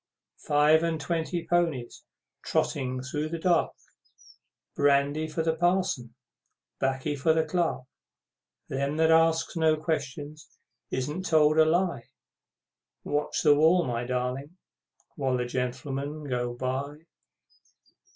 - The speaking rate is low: Yes, slow, 115 wpm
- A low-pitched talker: No, medium, 150 Hz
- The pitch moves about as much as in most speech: Yes, average, 3.4 semitones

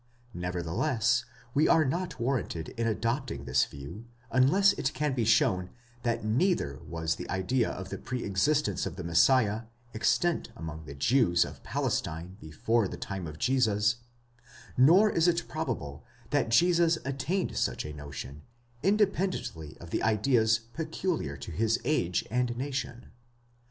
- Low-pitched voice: Yes, low, 115 Hz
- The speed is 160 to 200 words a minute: No, average, 145 wpm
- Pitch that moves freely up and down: Yes, wide, 8.0 semitones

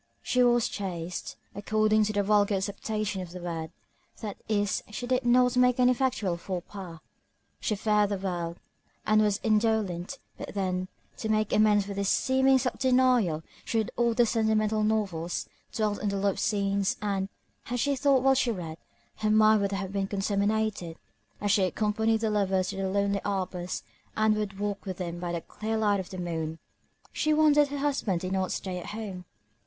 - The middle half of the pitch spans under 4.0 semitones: Yes, narrow, 2.6 semitones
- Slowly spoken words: No, average, 185 wpm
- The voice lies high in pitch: Yes, high, 205 Hz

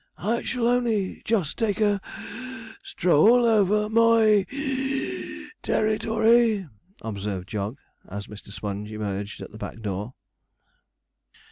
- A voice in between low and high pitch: No, high, 210 Hz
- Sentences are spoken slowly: Yes, slow, 130 wpm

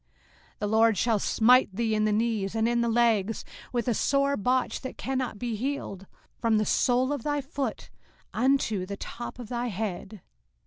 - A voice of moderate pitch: No, high, 230 Hz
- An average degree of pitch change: Yes, average, 3.0 semitones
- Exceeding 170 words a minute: Yes, average, 185 wpm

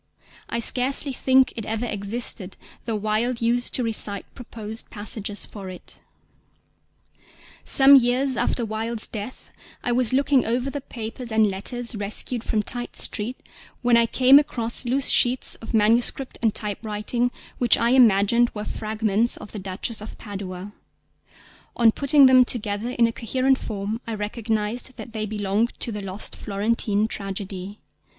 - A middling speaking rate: Yes, average, 150 wpm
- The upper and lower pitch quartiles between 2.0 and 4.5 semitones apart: Yes, average, 2.7 semitones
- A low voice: No, high, 225 Hz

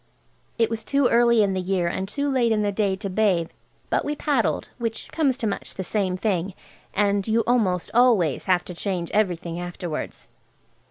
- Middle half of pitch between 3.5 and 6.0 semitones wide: Yes, average, 4.0 semitones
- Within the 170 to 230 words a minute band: Yes, average, 185 wpm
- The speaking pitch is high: Yes, high, 205 Hz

